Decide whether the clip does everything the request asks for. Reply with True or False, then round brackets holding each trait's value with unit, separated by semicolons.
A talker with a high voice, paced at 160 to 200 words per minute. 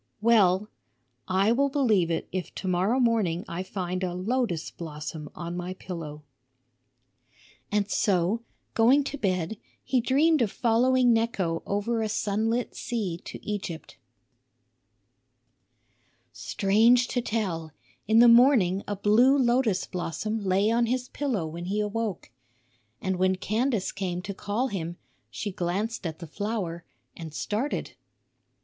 False (205 Hz; 135 wpm)